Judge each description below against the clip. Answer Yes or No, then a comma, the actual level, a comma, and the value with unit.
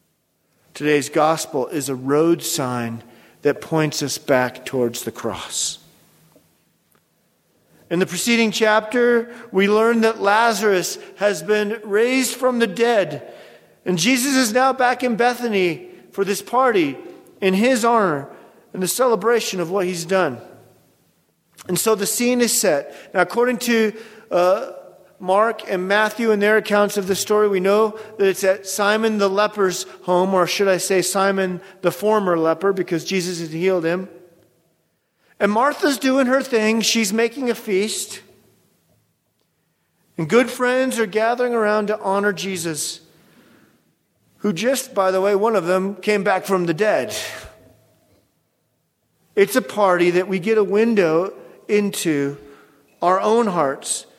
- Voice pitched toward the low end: No, high, 200 Hz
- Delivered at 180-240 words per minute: No, average, 145 wpm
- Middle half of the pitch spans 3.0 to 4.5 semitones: Yes, average, 4.1 semitones